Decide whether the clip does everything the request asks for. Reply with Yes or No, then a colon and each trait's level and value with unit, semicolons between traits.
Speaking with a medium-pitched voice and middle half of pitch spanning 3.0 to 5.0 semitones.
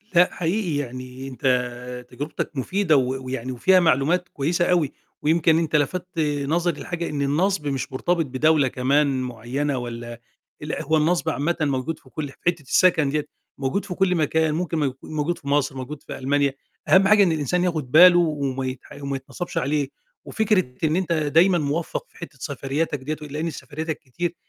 Yes: medium, 150 Hz; average, 4.1 semitones